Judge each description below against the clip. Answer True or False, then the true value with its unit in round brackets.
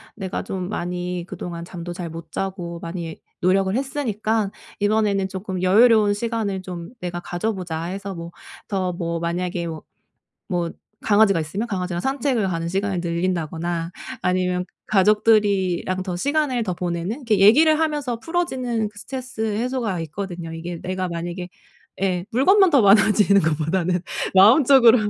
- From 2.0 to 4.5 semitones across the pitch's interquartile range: True (4.0 semitones)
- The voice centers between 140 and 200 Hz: True (190 Hz)